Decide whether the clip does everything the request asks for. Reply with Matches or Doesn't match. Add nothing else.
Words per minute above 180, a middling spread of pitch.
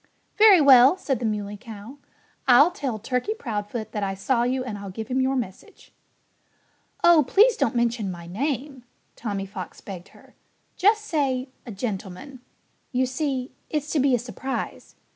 Doesn't match